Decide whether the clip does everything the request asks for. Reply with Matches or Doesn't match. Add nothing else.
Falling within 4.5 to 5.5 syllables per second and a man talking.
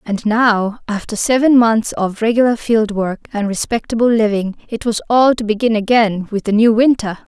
Doesn't match